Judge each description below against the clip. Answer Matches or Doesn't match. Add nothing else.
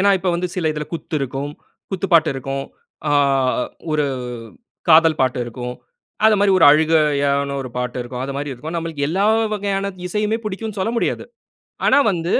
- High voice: Doesn't match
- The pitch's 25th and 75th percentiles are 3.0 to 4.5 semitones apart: Doesn't match